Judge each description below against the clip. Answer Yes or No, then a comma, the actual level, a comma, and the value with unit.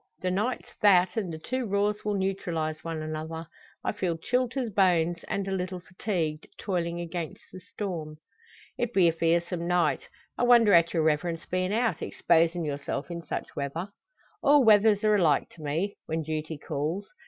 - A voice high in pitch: No, medium, 175 Hz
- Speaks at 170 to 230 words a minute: Yes, average, 175 wpm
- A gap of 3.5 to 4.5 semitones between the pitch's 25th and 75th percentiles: Yes, average, 3.8 semitones